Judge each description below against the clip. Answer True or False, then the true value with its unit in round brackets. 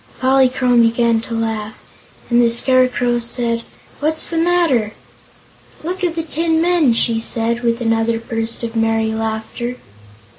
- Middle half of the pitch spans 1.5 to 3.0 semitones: True (2.7 semitones)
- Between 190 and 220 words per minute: False (140 wpm)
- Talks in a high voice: True (235 Hz)